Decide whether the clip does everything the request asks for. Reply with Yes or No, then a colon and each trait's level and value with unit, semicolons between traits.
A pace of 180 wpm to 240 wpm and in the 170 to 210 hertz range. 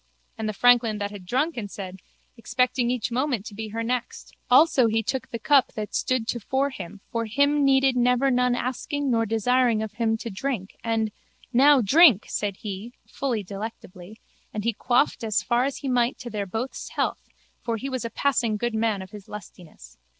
No: average, 190 wpm; high, 230 Hz